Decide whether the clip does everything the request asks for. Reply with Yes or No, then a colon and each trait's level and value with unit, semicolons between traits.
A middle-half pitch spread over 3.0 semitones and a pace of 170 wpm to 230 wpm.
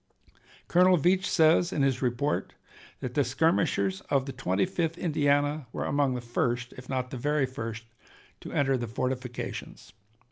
No: average, 3.7 semitones; average, 155 wpm